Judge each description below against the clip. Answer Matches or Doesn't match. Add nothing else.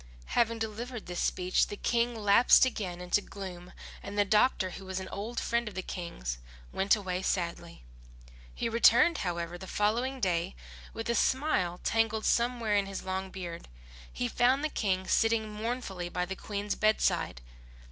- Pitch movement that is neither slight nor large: Matches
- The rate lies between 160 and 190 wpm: Matches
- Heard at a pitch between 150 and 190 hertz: Doesn't match